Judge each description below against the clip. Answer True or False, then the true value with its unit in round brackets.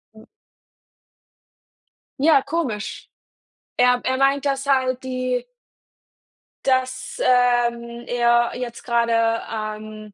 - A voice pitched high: True (245 Hz)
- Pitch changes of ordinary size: False (1.7 semitones)